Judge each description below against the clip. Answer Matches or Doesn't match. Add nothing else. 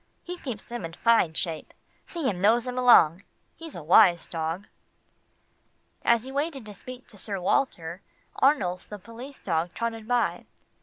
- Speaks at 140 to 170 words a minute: Matches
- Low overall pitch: Doesn't match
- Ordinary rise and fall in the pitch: Doesn't match